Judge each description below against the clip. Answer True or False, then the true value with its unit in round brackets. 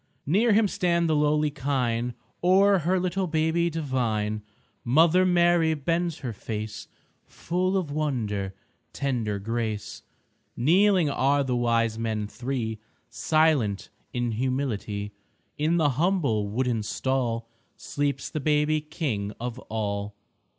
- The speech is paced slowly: True (120 wpm)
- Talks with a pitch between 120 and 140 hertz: True (135 Hz)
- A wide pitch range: True (6.3 semitones)